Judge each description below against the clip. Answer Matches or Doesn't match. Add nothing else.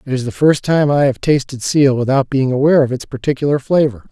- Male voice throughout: Matches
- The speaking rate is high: Matches